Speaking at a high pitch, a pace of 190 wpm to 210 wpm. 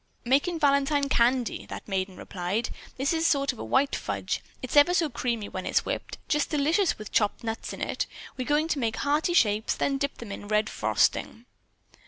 Yes: very high, 265 Hz; average, 200 wpm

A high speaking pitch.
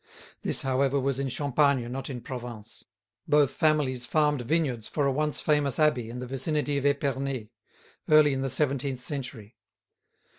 No: low, 135 Hz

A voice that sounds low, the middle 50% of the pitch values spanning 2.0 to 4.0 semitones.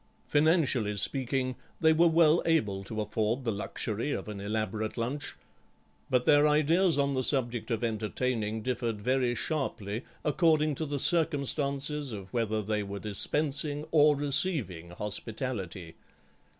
No: low, 130 Hz; wide, 5.5 semitones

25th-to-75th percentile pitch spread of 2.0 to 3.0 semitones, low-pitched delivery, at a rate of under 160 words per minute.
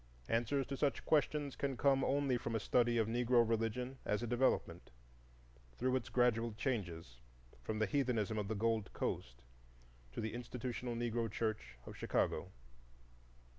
Yes: average, 2.7 semitones; low, 120 Hz; average, 150 wpm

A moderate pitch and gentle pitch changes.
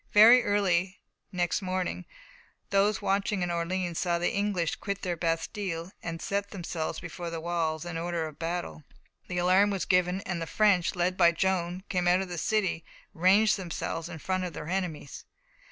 Yes: medium, 180 Hz; narrow, 2.3 semitones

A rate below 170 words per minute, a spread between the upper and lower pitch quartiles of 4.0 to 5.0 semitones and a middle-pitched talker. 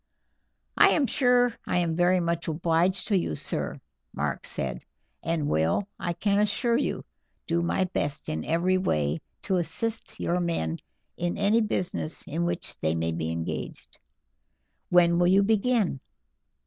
Yes: average, 150 wpm; average, 4.5 semitones; medium, 175 Hz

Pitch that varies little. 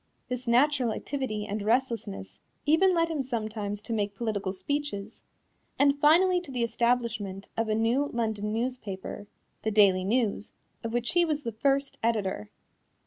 No: average, 4.7 semitones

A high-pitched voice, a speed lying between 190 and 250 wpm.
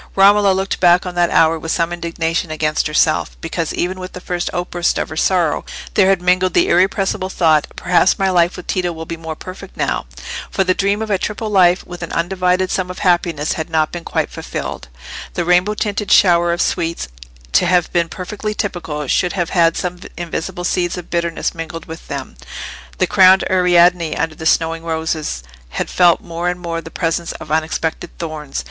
No: medium, 175 Hz; average, 195 wpm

